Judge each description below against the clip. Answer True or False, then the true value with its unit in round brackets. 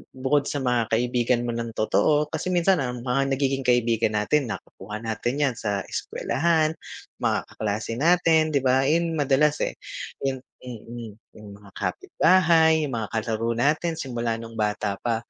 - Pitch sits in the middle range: False (125 Hz)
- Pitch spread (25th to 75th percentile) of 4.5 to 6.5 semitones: True (4.8 semitones)